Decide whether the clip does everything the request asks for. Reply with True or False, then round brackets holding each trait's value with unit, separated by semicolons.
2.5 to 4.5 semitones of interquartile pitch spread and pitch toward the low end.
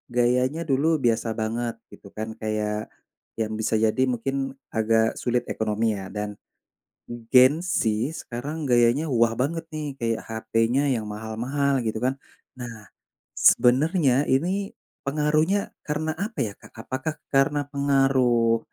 True (3.8 semitones; 125 Hz)